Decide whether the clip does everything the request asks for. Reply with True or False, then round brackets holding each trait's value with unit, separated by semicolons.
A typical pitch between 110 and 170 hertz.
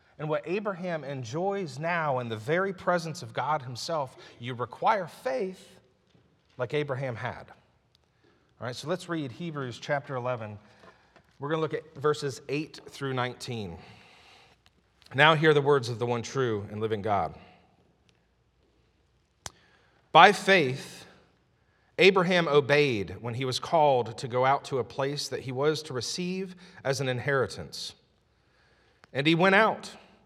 True (140 Hz)